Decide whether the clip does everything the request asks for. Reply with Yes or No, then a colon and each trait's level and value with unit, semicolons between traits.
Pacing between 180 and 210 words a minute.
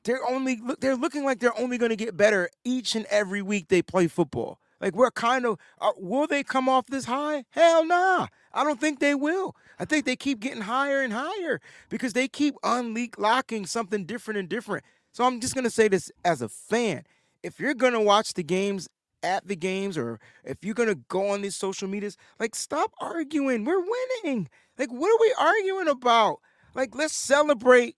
Yes: average, 200 wpm